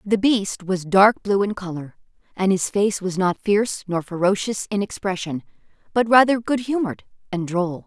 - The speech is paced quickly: No, average, 175 wpm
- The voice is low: No, high, 200 Hz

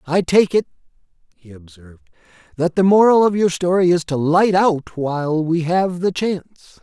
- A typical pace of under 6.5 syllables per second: Yes, 5.1 syllables/s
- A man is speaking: Yes, male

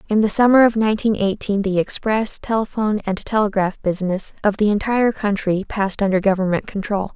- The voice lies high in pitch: Yes, high, 205 Hz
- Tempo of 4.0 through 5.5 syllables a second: No, 5.9 syllables/s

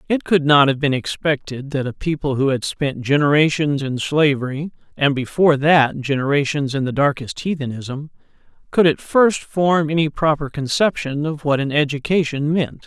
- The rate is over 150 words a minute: Yes, average, 165 wpm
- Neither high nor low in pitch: Yes, medium, 145 Hz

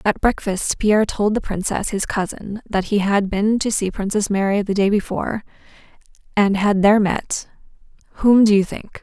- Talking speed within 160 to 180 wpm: Yes, average, 175 wpm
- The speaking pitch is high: Yes, high, 205 Hz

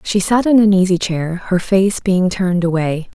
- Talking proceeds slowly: No, fast, 205 wpm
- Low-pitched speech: No, medium, 185 Hz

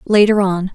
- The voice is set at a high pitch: Yes, high, 200 Hz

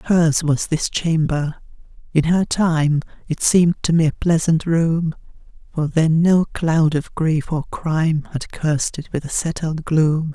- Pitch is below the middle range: No, medium, 160 Hz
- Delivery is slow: No, average, 170 wpm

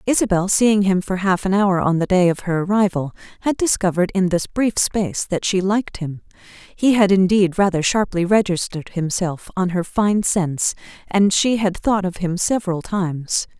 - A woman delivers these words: Yes, female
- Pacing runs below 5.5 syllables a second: Yes, 5.1 syllables/s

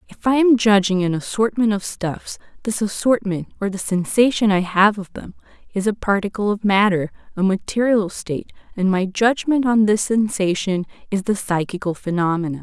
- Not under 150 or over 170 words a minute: Yes, average, 165 wpm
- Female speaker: Yes, female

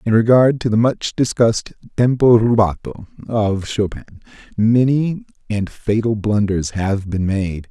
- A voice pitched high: No, low, 110 Hz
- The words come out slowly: Yes, slow, 130 wpm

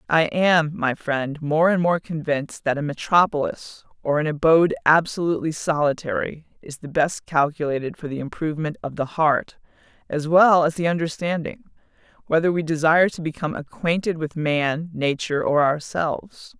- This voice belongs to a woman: Yes, female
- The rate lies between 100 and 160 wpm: Yes, average, 150 wpm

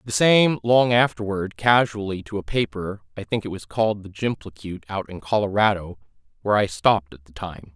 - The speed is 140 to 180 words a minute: Yes, average, 170 wpm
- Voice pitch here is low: Yes, low, 100 Hz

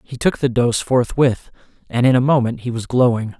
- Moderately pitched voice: No, low, 125 Hz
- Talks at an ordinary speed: No, fast, 210 wpm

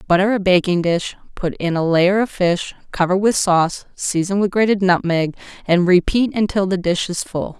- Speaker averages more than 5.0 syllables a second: No, 4.9 syllables/s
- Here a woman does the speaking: Yes, female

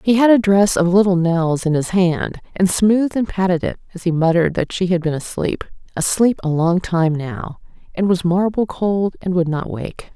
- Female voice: Yes, female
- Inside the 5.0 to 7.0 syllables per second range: No, 4.8 syllables/s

